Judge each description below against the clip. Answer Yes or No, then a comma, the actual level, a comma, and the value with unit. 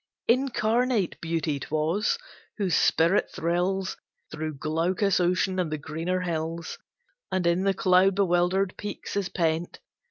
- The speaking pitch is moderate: Yes, medium, 180 Hz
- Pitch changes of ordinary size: Yes, average, 3.0 semitones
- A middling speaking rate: No, slow, 125 wpm